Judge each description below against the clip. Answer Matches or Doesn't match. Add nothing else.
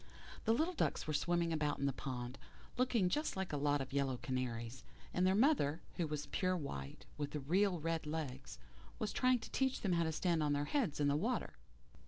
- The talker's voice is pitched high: Doesn't match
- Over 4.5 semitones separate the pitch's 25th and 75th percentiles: Matches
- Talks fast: Matches